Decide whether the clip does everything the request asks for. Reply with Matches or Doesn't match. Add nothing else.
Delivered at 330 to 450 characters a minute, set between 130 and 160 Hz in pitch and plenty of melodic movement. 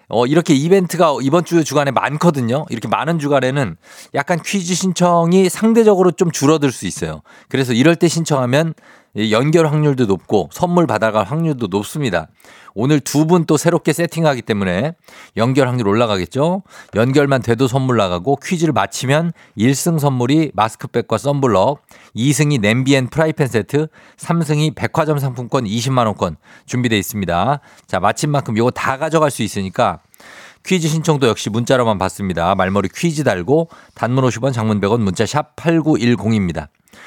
Matches